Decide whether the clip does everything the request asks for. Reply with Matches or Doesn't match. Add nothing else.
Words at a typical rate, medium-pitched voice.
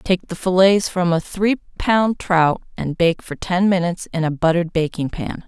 Matches